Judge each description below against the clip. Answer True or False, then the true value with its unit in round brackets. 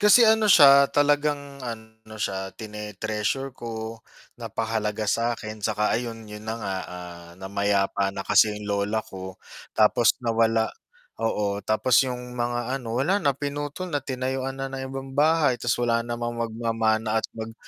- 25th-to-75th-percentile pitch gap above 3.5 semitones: True (3.9 semitones)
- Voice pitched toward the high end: False (115 Hz)